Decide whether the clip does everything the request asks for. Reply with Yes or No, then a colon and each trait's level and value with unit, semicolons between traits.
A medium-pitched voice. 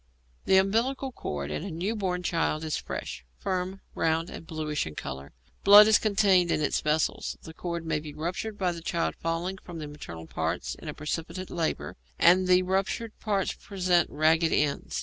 Yes: medium, 170 Hz